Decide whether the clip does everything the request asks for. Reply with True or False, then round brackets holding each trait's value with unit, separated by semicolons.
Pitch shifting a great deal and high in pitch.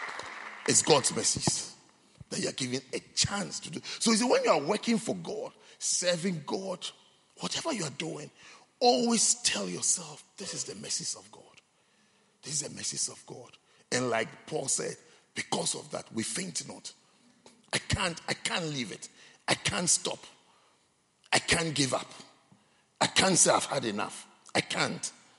True (6.2 semitones; 200 Hz)